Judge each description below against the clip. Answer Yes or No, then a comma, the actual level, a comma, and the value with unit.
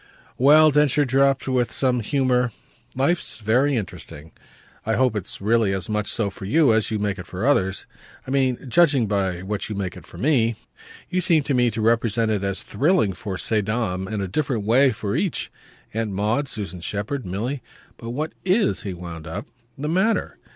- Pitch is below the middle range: Yes, low, 115 Hz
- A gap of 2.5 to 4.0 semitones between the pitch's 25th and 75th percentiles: No, average, 5.3 semitones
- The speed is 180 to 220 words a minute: Yes, average, 190 wpm